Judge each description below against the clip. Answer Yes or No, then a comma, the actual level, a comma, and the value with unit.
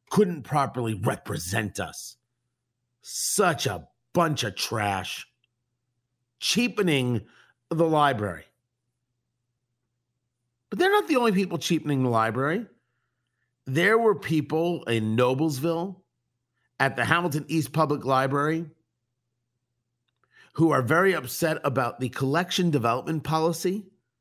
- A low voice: Yes, low, 130 Hz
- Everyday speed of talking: No, slow, 100 wpm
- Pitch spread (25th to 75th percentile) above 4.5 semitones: Yes, average, 5.0 semitones